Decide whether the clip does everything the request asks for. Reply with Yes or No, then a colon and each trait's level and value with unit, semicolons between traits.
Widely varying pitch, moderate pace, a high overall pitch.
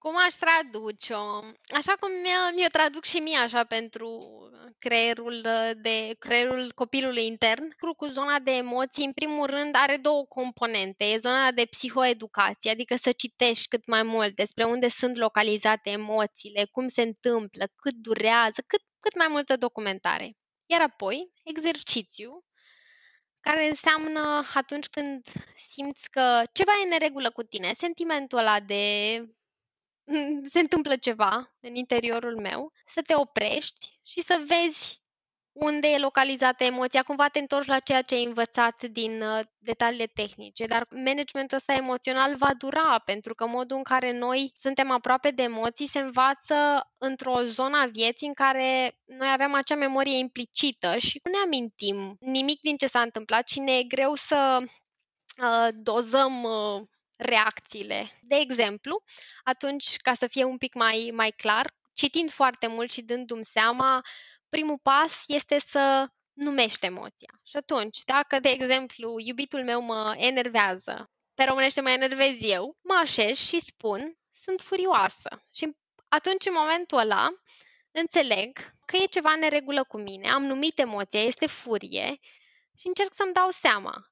No: average, 4.1 semitones; average, 150 wpm; very high, 260 Hz